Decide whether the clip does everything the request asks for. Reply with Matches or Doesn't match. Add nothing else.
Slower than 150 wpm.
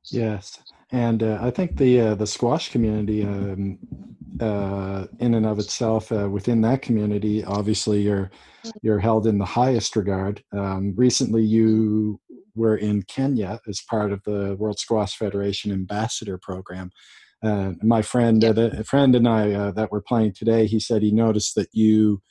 Doesn't match